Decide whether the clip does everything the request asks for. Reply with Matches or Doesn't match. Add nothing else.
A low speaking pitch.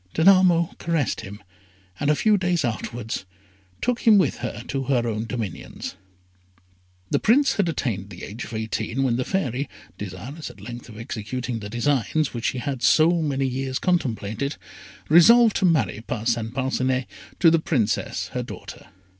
Matches